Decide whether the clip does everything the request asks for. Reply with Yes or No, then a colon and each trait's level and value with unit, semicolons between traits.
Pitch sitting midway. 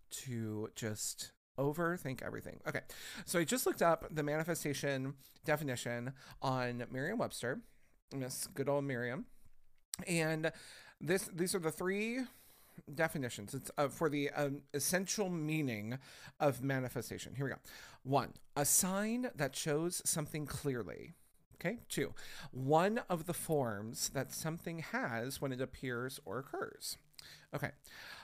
Yes: medium, 145 Hz